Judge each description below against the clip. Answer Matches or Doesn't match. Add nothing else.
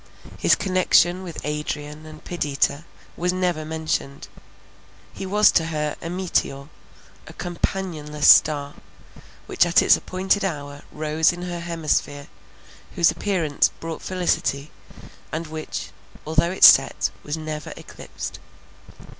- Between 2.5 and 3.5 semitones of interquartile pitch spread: Matches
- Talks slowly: Matches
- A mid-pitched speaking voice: Matches